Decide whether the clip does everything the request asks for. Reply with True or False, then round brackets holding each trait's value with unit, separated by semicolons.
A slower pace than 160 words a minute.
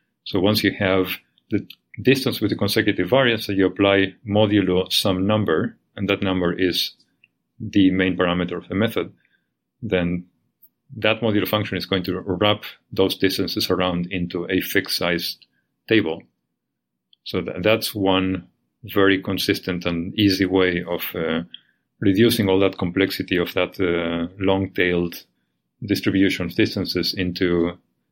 True (145 wpm)